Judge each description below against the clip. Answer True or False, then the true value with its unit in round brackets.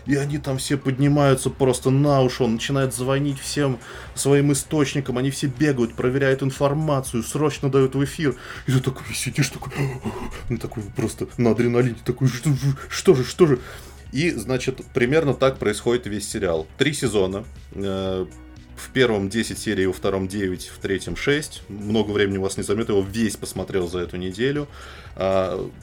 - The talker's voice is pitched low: True (130 Hz)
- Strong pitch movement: False (4.8 semitones)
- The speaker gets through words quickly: True (165 wpm)